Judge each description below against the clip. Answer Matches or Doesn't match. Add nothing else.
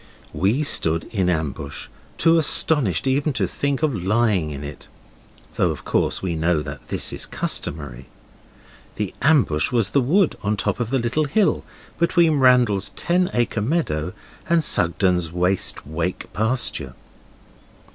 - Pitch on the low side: Matches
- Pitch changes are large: Matches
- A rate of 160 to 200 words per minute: Doesn't match